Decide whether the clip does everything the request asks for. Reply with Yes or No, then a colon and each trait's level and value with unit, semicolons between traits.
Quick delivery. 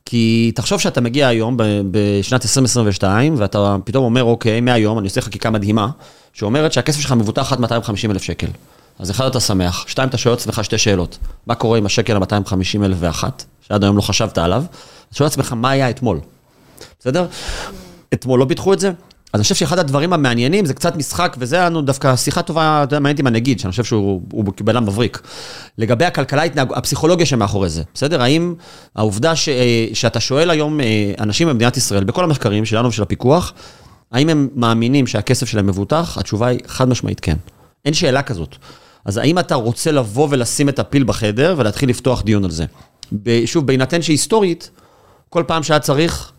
Yes: fast, 180 wpm